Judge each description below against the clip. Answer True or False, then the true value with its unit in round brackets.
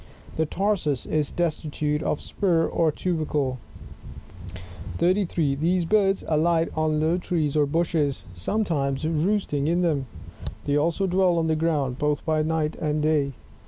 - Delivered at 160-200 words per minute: False (145 wpm)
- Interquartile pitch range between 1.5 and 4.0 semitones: True (2.6 semitones)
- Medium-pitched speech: True (155 Hz)